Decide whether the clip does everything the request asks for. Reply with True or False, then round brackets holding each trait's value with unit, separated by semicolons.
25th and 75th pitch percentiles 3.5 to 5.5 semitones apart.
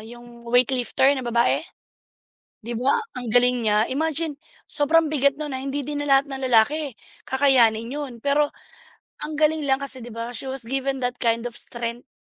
False (3.1 semitones)